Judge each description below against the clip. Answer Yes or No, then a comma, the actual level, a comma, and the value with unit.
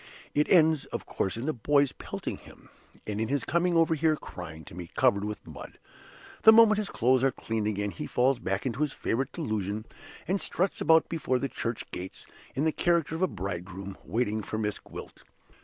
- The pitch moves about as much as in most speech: No, wide, 7.4 semitones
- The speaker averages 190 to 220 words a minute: Yes, average, 195 wpm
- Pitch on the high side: No, low, 125 Hz